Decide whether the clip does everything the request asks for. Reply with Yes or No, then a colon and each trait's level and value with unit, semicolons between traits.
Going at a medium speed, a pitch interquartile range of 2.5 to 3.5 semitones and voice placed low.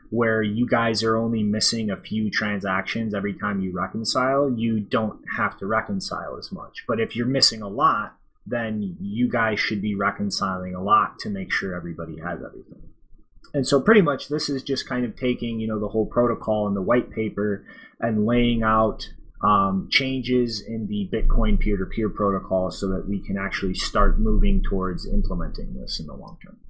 Yes: average, 185 wpm; average, 2.9 semitones; low, 110 Hz